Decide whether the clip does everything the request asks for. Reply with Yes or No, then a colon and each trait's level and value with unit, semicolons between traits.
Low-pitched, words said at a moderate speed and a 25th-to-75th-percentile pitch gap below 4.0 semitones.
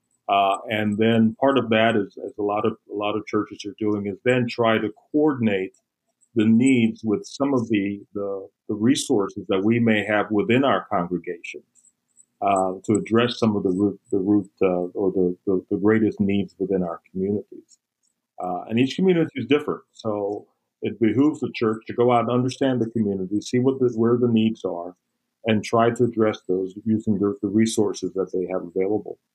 Yes: low, 110 Hz; average, 190 wpm; average, 2.9 semitones